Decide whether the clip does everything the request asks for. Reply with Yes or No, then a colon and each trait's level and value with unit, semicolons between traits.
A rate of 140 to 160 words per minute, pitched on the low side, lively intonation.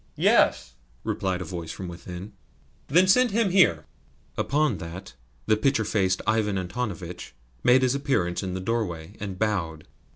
Yes: average, 150 wpm; low, 100 Hz; wide, 5.7 semitones